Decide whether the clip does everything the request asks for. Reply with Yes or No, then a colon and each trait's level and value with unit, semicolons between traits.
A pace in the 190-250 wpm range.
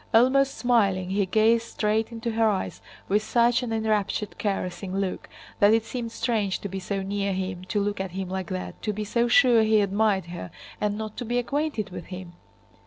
Yes: average, 200 wpm